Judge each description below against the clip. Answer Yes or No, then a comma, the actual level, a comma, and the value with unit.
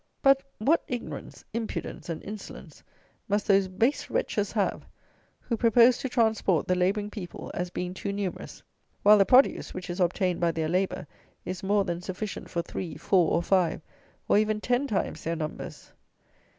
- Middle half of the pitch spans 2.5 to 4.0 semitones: Yes, average, 3.4 semitones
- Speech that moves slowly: No, average, 165 wpm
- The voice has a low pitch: No, high, 195 Hz